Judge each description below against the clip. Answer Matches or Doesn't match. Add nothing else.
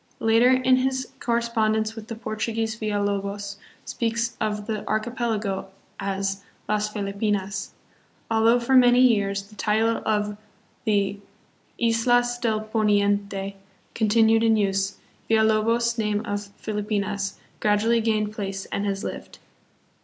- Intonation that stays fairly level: Matches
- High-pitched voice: Matches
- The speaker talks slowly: Matches